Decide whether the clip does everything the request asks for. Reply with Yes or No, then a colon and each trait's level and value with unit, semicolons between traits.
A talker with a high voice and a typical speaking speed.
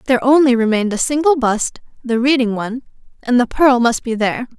Yes: high, 245 Hz; average, 170 wpm